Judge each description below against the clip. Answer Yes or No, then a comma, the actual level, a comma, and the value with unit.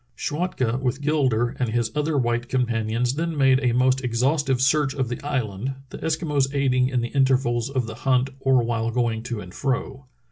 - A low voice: Yes, low, 130 Hz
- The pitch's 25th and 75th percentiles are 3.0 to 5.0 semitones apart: No, narrow, 2.4 semitones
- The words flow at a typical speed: Yes, average, 185 wpm